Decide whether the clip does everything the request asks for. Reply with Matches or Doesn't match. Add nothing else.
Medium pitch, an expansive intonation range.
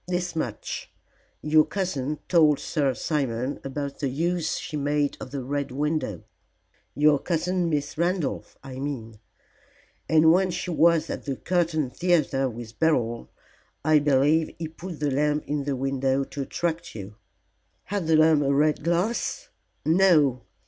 Doesn't match